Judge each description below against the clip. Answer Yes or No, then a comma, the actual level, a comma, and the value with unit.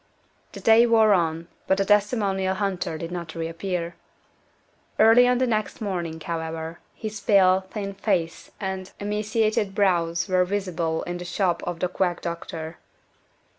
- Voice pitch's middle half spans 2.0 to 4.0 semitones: Yes, average, 3.5 semitones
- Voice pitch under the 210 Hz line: Yes, medium, 185 Hz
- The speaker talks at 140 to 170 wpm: Yes, average, 145 wpm